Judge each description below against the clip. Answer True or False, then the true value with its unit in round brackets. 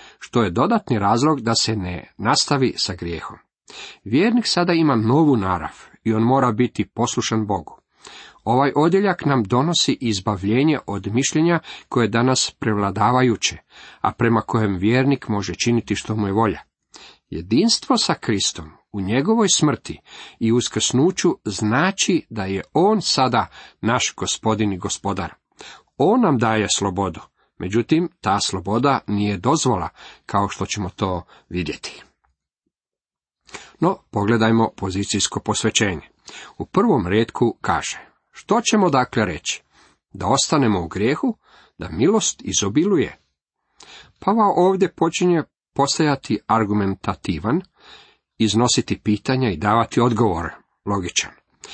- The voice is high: False (115 Hz)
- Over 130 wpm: False (120 wpm)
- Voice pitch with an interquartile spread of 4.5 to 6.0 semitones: True (5.1 semitones)